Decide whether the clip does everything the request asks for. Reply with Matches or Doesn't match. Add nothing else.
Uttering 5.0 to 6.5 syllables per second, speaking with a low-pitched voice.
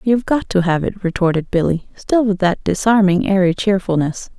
Doesn't match